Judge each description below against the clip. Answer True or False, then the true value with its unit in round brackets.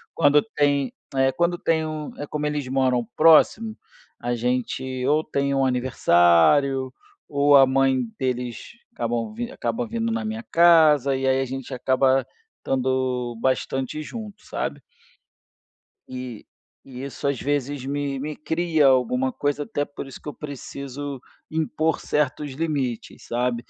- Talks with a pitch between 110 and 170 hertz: True (140 Hz)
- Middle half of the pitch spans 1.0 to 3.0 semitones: True (2.7 semitones)